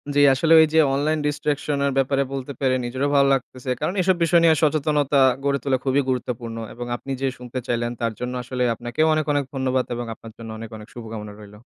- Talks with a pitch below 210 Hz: Yes, low, 135 Hz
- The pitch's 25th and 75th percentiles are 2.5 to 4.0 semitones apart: Yes, average, 3.2 semitones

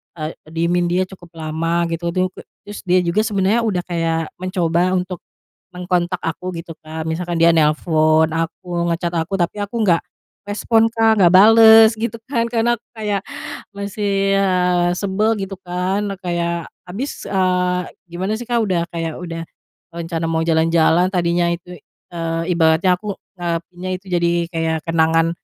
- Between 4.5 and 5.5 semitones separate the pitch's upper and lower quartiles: No, average, 2.8 semitones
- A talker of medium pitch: Yes, medium, 175 Hz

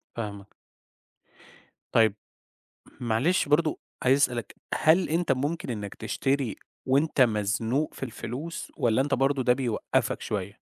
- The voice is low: Yes, low, 130 Hz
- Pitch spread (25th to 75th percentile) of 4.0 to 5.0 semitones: Yes, average, 4.3 semitones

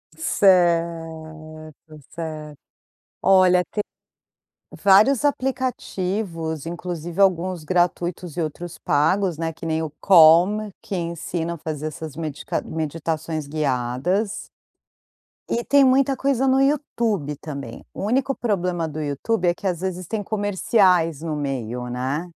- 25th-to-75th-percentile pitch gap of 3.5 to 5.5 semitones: Yes, average, 4.1 semitones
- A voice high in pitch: No, medium, 170 Hz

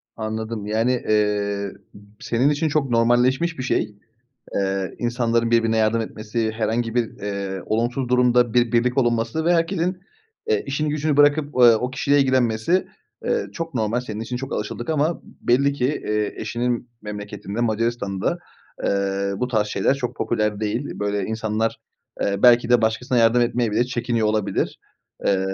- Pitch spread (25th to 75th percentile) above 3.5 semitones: No, average, 2.9 semitones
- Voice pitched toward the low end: Yes, low, 115 Hz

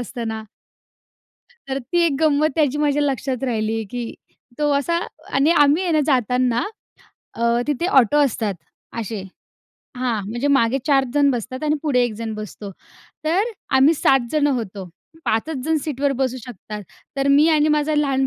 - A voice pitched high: Yes, very high, 270 Hz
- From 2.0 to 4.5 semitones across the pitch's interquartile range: Yes, average, 4.2 semitones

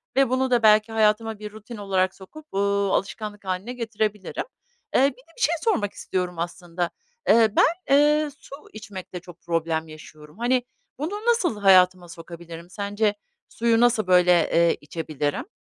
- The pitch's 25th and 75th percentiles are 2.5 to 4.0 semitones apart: No, average, 5.1 semitones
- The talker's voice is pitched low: No, high, 205 Hz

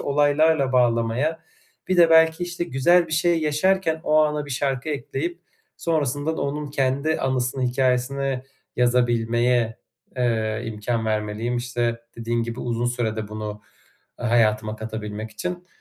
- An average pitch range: Yes, average, 4.8 semitones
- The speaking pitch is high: No, low, 125 Hz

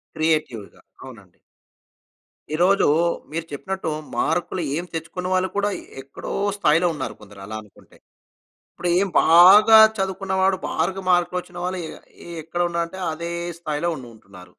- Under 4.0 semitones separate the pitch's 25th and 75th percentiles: No, average, 4.3 semitones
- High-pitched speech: No, medium, 170 Hz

